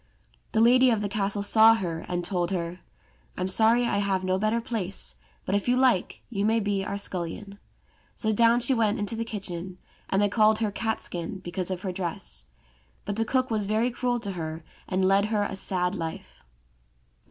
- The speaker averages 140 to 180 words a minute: No, average, 195 wpm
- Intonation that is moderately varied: Yes, average, 3.4 semitones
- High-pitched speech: Yes, high, 200 Hz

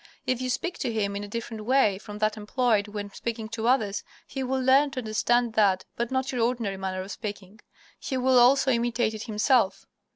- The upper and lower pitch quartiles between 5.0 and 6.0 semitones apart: No, average, 3.5 semitones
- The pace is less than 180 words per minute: No, fast, 205 wpm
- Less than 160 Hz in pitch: No, high, 230 Hz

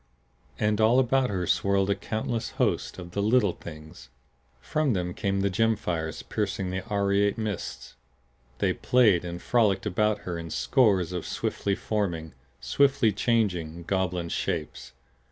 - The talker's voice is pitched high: No, low, 100 Hz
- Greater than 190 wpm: No, average, 145 wpm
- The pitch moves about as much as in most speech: Yes, average, 3.8 semitones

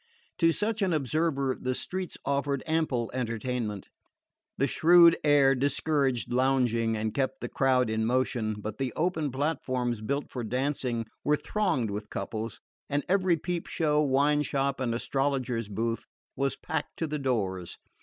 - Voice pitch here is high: No, low, 135 Hz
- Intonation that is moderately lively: Yes, average, 4.0 semitones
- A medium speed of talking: Yes, average, 150 wpm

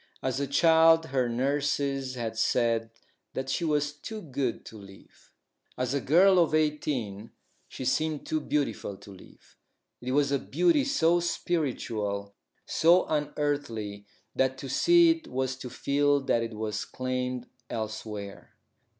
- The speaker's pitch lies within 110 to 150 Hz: Yes, low, 135 Hz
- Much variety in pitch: No, average, 4.9 semitones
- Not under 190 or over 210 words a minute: No, average, 140 wpm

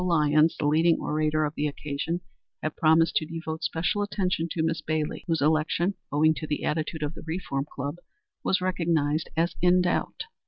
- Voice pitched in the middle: Yes, medium, 160 Hz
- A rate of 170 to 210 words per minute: Yes, average, 180 wpm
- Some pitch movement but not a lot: No, narrow, 1.8 semitones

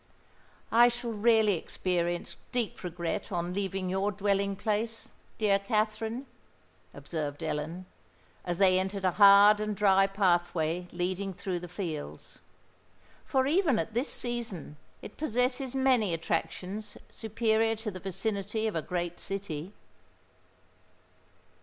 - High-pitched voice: Yes, high, 200 Hz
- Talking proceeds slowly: Yes, slow, 120 wpm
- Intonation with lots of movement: No, average, 3.8 semitones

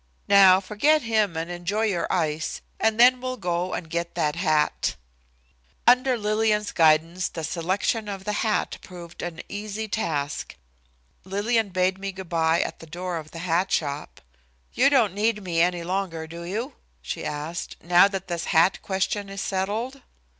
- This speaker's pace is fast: No, average, 165 wpm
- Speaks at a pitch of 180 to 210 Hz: Yes, medium, 185 Hz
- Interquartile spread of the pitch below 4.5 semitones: Yes, average, 3.8 semitones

